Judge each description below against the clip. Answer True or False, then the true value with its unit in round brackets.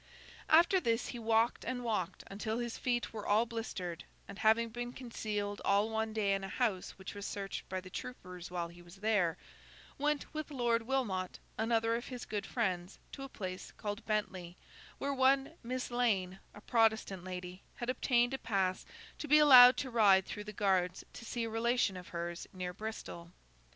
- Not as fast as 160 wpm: False (185 wpm)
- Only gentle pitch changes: False (4.3 semitones)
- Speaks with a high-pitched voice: True (220 Hz)